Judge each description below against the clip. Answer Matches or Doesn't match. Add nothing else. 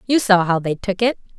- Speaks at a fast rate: Matches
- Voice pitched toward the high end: Matches